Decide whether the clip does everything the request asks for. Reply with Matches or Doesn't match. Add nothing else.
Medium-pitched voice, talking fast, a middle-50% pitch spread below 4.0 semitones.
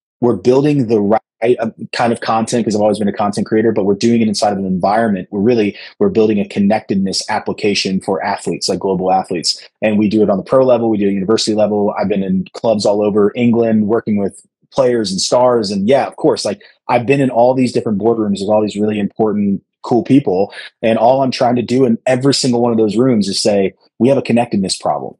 Doesn't match